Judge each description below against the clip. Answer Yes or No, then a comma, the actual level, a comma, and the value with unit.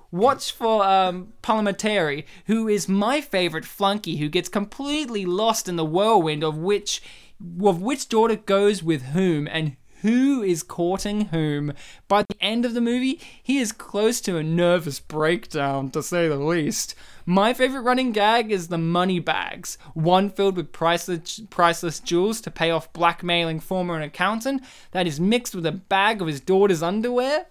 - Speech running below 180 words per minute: Yes, average, 165 wpm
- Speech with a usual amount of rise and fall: Yes, average, 4.4 semitones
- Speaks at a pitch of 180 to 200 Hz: Yes, high, 190 Hz